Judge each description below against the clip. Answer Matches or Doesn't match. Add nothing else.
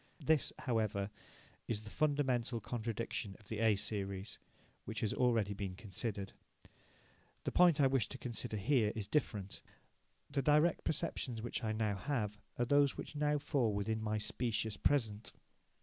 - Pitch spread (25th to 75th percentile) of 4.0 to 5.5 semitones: Matches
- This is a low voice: Matches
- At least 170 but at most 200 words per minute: Doesn't match